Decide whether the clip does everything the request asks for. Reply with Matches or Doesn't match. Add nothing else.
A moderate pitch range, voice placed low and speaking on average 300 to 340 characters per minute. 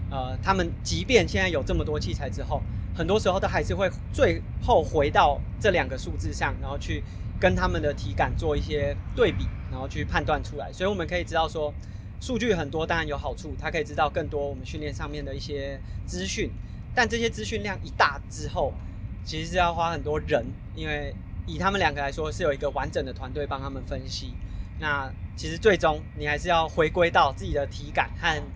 Doesn't match